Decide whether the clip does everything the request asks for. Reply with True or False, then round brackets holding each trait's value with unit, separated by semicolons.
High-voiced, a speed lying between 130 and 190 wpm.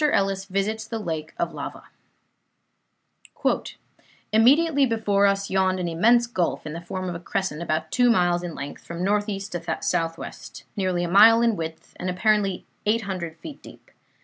True (195 Hz; 160 wpm)